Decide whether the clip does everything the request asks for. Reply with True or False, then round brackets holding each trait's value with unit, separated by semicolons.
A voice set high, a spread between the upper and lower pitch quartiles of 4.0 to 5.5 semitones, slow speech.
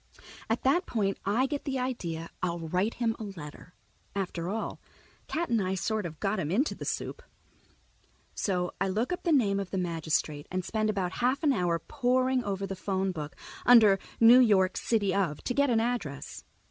False (200 Hz; 5.2 semitones; 190 wpm)